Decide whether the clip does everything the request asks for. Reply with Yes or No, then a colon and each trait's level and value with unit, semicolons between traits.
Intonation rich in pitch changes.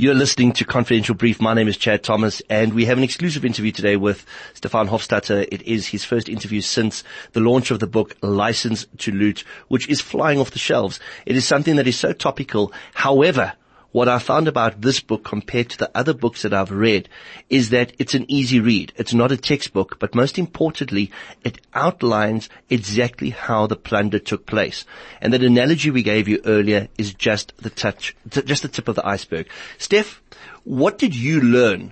No: average, 4.0 semitones